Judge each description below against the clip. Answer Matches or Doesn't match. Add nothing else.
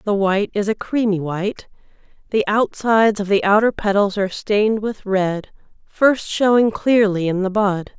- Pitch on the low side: Doesn't match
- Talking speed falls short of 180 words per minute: Matches